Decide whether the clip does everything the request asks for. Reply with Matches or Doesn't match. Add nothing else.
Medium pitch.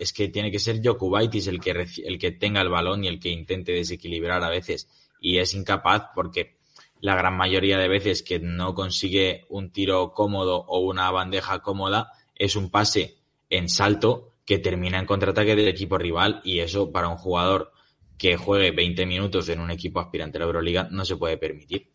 Doesn't match